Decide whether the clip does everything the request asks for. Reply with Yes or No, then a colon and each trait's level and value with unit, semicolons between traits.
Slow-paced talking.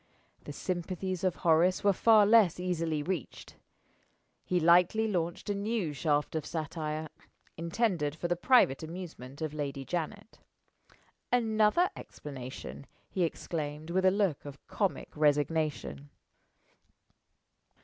Yes: slow, 120 wpm